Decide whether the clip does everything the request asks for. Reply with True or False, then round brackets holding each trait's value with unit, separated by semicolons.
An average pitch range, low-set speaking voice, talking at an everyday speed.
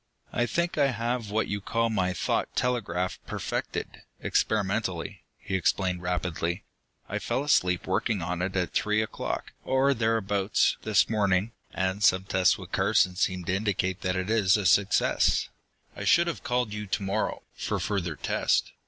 True (3.4 semitones; 100 Hz; 160 wpm)